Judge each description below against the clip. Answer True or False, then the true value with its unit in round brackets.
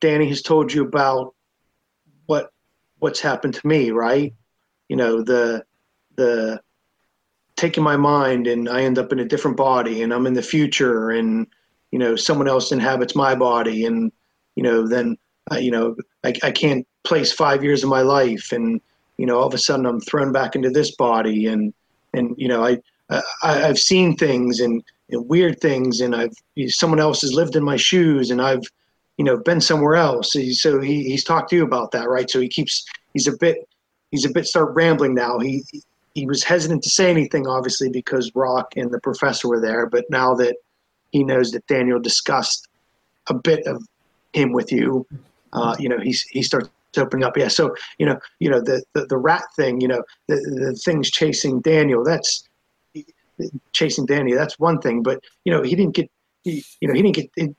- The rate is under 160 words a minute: False (205 wpm)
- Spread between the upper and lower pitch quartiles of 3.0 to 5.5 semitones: True (3.8 semitones)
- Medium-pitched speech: False (130 Hz)